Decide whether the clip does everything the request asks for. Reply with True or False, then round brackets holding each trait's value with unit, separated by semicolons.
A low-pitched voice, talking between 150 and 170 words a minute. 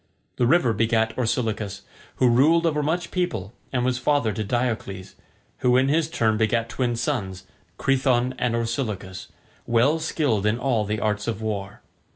True (120 Hz; 160 wpm)